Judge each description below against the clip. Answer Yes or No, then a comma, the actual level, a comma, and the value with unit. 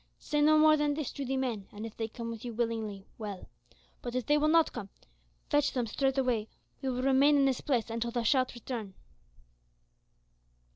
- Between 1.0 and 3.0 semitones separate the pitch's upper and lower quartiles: No, average, 3.8 semitones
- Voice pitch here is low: No, very high, 250 Hz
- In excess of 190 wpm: Yes, average, 200 wpm